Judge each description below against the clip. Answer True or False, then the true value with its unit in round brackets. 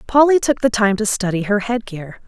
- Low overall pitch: False (220 Hz)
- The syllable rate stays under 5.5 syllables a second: True (5.2 syllables/s)